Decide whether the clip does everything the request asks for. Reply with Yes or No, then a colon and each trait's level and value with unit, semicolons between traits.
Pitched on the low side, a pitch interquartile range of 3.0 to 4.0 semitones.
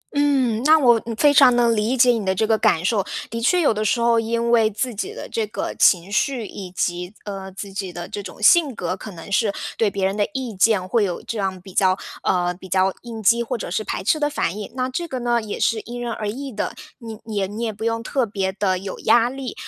No: high, 220 Hz; average, 3.7 semitones